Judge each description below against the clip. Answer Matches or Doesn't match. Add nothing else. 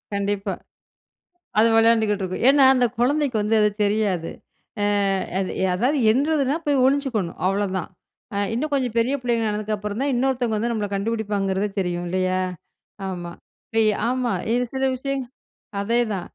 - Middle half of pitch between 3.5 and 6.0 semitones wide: Matches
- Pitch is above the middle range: Matches